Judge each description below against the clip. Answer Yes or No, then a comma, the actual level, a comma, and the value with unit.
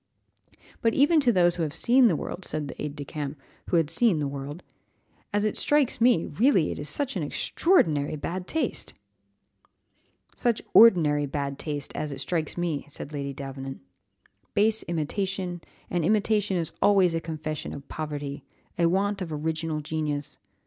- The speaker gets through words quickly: No, average, 165 wpm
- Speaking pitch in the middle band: Yes, medium, 165 Hz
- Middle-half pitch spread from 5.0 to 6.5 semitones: Yes, wide, 5.5 semitones